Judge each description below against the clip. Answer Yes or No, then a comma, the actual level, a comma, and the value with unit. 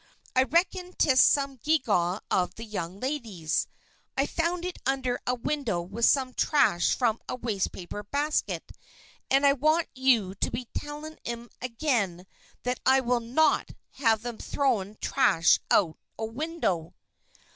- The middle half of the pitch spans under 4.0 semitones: No, wide, 5.5 semitones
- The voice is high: Yes, very high, 250 Hz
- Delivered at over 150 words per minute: No, average, 145 wpm